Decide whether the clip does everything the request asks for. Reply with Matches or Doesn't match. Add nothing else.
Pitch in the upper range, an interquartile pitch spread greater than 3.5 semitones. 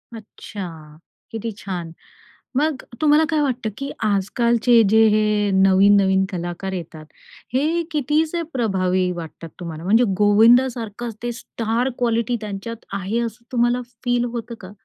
Matches